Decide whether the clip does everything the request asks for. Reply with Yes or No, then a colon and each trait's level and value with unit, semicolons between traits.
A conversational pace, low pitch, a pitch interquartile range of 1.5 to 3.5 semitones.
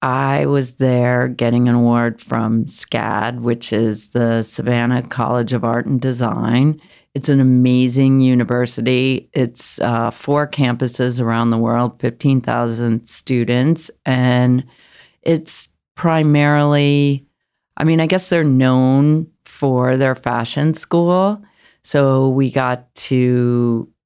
No: slow, 115 wpm; low, 125 Hz; average, 2.8 semitones